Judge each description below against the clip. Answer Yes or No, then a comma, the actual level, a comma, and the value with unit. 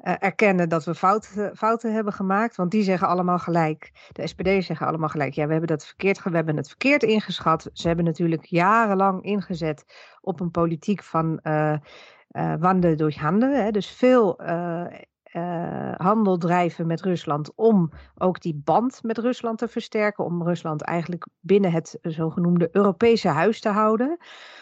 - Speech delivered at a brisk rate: No, average, 165 wpm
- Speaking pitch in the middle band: Yes, medium, 180 Hz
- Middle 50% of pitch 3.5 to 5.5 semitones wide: Yes, average, 4.1 semitones